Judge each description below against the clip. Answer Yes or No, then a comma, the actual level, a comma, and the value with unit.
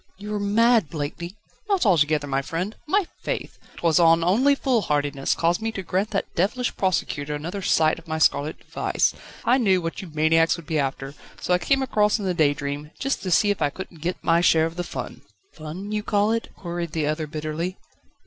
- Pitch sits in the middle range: Yes, medium, 170 Hz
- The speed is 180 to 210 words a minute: Yes, average, 200 wpm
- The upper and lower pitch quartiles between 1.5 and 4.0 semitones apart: No, average, 4.9 semitones